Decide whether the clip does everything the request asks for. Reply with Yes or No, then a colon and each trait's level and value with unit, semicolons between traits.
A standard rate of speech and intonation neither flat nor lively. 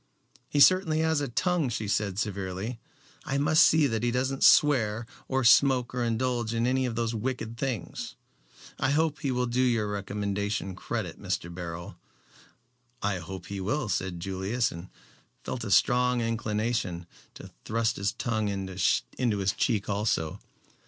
Yes: average, 160 wpm; average, 4.2 semitones